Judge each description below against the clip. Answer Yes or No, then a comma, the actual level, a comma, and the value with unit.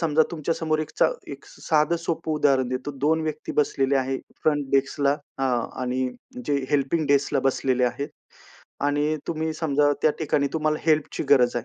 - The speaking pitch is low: No, medium, 145 Hz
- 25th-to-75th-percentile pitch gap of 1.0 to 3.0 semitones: Yes, narrow, 2.5 semitones